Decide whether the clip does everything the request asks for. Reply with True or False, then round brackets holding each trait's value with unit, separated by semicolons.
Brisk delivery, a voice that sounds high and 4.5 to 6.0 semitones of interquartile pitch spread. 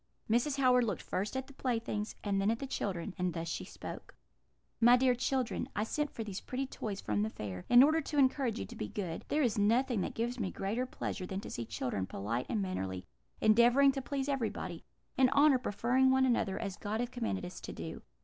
True (220 wpm; 230 Hz; 5.2 semitones)